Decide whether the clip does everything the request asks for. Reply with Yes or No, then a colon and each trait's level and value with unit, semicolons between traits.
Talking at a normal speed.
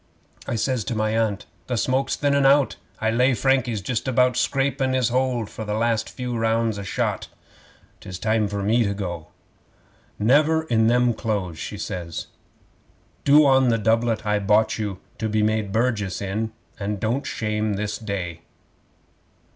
Yes: average, 165 wpm